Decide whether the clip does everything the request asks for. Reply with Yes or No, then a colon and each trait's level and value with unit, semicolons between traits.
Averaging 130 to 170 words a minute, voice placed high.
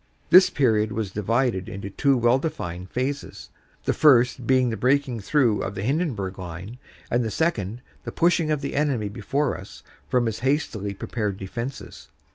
No: average, 165 wpm; low, 120 Hz